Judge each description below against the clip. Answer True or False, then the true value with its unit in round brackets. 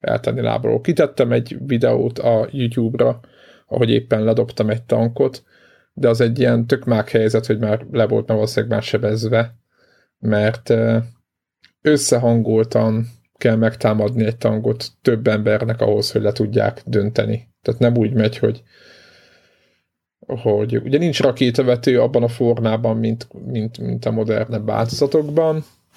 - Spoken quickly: False (130 wpm)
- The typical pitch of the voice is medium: False (115 Hz)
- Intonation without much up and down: True (1.7 semitones)